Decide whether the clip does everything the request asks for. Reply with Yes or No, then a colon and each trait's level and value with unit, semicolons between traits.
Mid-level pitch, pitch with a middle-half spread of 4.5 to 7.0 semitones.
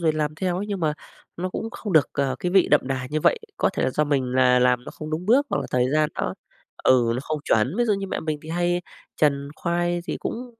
Yes: medium, 155 Hz; average, 4.9 semitones